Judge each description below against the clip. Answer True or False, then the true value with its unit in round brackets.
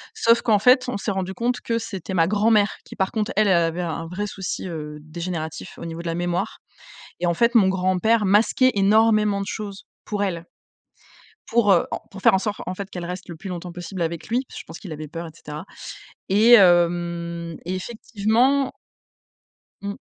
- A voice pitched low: False (190 Hz)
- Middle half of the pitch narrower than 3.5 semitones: False (3.8 semitones)